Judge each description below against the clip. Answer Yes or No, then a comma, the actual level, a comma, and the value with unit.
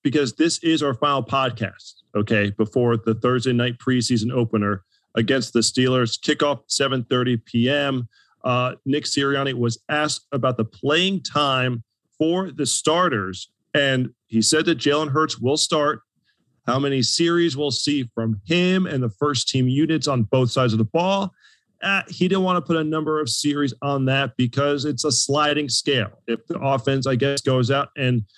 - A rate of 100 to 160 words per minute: No, average, 175 wpm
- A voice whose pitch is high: No, low, 135 Hz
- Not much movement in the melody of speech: No, average, 3.8 semitones